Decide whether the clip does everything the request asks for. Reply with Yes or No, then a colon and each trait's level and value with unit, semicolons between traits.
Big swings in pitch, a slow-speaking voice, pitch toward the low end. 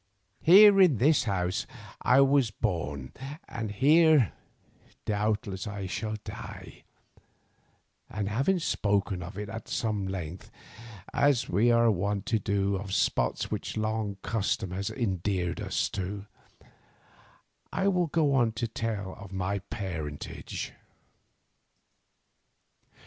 No: average, 3.8 semitones; slow, 115 wpm; low, 105 Hz